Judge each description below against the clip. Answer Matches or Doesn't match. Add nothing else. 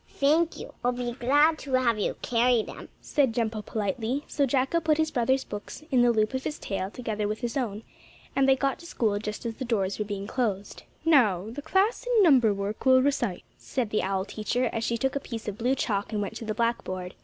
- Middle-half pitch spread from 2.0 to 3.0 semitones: Doesn't match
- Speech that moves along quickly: Matches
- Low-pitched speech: Doesn't match